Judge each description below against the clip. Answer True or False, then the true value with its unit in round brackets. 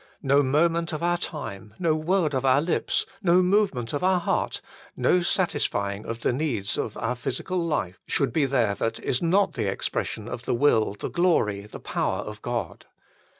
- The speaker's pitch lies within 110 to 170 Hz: True (140 Hz)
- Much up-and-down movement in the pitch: True (7.2 semitones)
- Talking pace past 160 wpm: True (185 wpm)